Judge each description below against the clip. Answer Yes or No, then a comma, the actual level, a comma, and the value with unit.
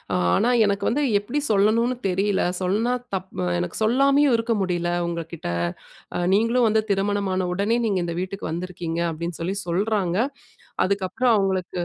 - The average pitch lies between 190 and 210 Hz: Yes, high, 195 Hz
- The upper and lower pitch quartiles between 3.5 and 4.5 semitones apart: Yes, average, 3.8 semitones